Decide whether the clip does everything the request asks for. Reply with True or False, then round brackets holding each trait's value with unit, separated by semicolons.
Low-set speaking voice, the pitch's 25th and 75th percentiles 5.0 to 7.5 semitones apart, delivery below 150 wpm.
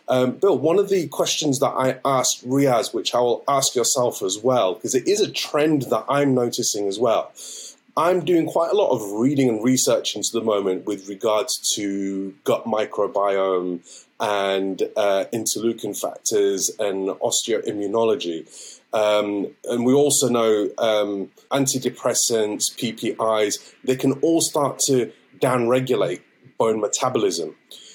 True (120 Hz; 5.5 semitones; 140 wpm)